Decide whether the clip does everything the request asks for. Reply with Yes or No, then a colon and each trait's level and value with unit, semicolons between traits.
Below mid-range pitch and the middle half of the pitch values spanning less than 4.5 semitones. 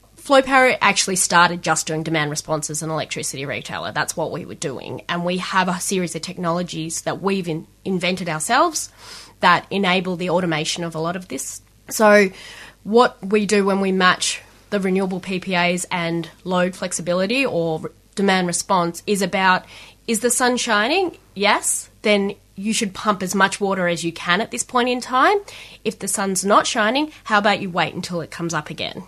No: medium, 185 Hz; average, 3.5 semitones